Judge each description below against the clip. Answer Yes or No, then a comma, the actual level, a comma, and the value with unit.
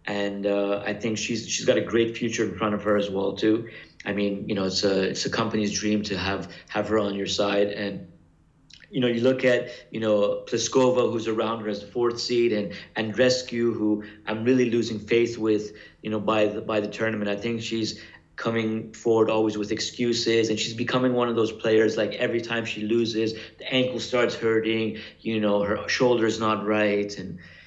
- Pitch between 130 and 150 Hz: No, low, 110 Hz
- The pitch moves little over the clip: Yes, narrow, 1.9 semitones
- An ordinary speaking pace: No, fast, 210 wpm